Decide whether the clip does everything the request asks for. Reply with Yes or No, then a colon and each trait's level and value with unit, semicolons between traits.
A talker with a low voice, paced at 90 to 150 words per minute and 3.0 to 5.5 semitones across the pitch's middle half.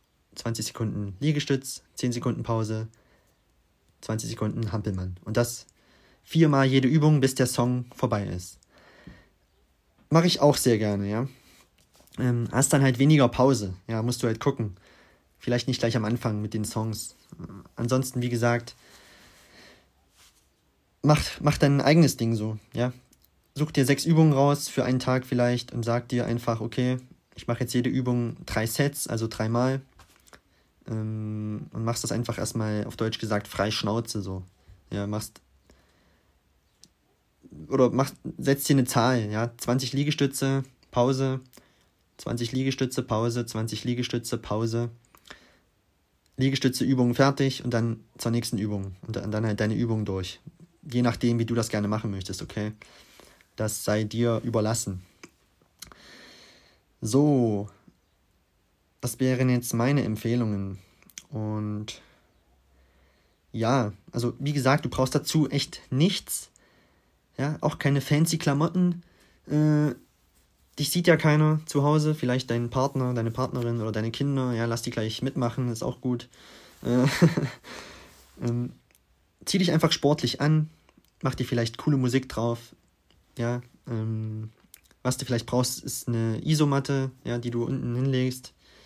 Yes: low, 120 Hz; average, 135 wpm; average, 3.9 semitones